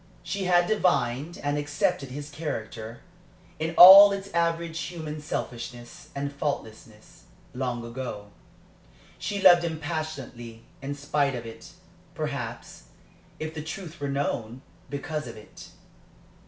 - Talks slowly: Yes, slow, 125 wpm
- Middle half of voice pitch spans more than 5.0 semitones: Yes, wide, 5.4 semitones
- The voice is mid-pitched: Yes, medium, 145 Hz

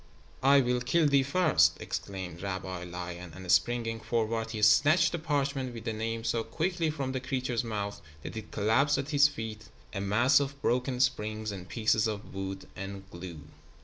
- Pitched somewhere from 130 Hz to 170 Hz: No, low, 115 Hz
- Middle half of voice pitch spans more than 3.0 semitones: Yes, wide, 5.4 semitones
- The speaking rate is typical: Yes, average, 180 wpm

